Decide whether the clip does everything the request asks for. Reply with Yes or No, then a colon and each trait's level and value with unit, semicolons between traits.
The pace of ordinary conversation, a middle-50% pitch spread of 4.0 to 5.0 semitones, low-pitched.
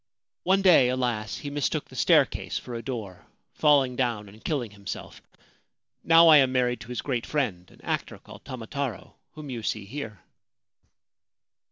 Yes: average, 160 wpm; average, 4.6 semitones; low, 125 Hz